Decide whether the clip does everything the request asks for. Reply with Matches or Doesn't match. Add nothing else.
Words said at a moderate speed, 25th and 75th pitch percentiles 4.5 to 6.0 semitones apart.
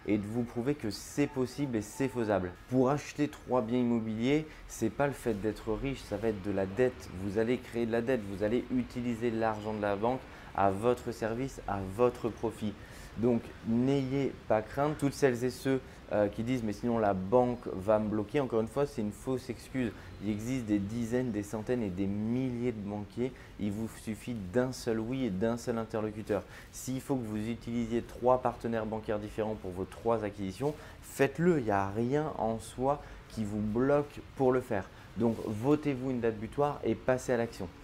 Doesn't match